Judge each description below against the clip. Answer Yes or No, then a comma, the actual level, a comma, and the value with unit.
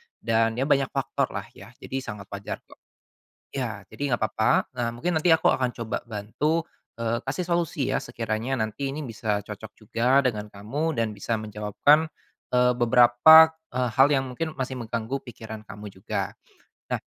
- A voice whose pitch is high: No, low, 120 Hz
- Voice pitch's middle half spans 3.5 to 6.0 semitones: Yes, average, 4.0 semitones